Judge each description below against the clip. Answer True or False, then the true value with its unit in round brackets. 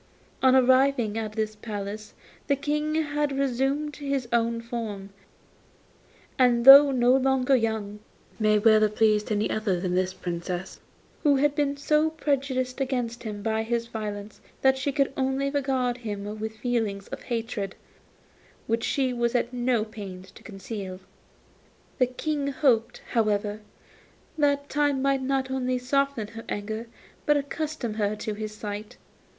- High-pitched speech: True (240 Hz)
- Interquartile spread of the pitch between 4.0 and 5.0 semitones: True (4.3 semitones)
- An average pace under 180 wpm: True (150 wpm)